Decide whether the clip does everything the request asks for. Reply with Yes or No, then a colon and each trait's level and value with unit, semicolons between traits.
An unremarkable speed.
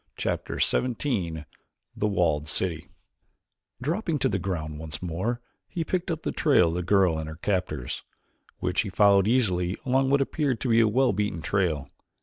Yes: average, 170 wpm